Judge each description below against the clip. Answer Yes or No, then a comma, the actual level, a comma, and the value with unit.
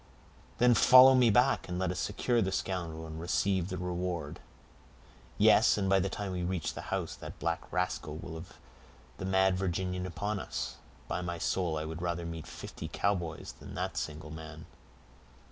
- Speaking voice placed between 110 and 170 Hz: No, very low, 90 Hz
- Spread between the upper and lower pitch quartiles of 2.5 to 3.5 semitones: Yes, average, 2.8 semitones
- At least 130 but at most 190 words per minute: Yes, average, 180 wpm